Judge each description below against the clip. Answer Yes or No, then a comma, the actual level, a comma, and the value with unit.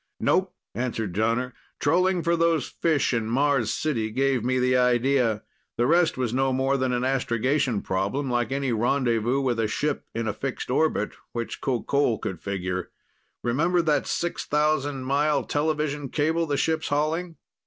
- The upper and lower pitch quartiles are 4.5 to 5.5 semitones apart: No, average, 4.0 semitones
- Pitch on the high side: No, low, 135 Hz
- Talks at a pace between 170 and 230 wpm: No, average, 155 wpm